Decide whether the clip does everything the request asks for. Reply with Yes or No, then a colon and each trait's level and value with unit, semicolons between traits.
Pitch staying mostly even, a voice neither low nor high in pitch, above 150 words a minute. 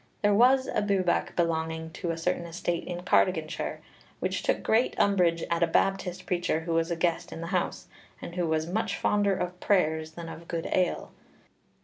Yes: narrow, 2.3 semitones; medium, 175 Hz; average, 190 wpm